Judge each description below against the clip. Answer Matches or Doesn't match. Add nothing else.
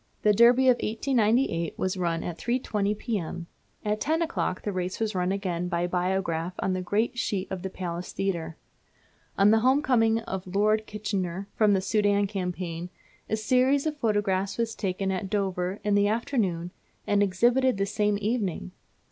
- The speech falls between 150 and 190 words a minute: Matches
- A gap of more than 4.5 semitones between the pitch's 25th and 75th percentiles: Doesn't match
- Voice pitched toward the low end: Doesn't match